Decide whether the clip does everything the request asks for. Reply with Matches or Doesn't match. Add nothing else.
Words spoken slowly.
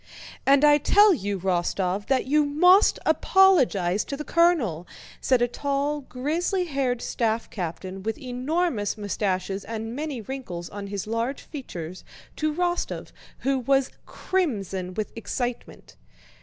Matches